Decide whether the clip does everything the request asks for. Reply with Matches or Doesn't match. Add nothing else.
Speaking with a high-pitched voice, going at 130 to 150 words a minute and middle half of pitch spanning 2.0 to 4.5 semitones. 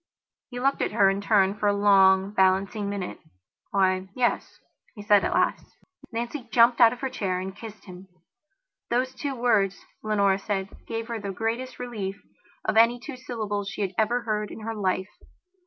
Doesn't match